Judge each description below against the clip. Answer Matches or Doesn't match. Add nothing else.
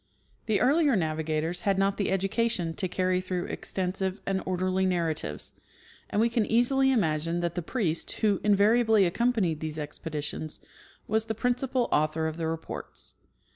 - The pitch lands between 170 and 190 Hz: Matches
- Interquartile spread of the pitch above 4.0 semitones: Matches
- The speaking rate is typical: Matches